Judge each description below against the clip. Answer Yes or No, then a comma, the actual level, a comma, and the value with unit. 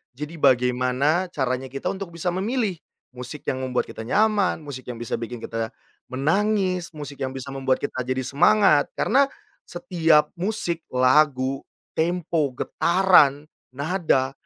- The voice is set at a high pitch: No, medium, 145 Hz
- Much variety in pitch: Yes, wide, 5.7 semitones